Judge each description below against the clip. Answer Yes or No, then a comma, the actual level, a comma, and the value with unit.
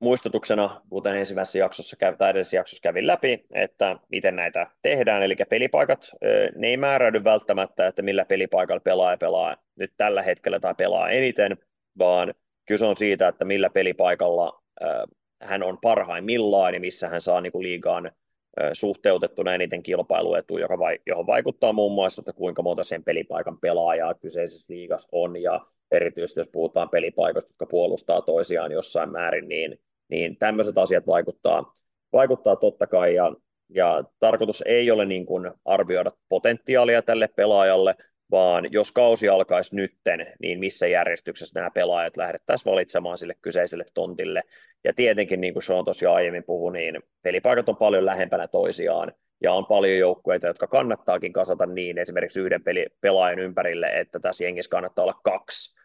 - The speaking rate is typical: Yes, average, 145 wpm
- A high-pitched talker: No, low, 130 Hz